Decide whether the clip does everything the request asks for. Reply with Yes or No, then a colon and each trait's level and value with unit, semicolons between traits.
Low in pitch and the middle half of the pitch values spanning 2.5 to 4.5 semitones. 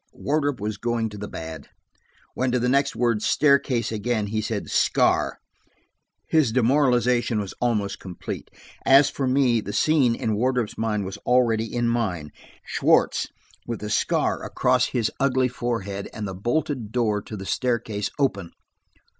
Yes: low, 115 Hz; average, 3.3 semitones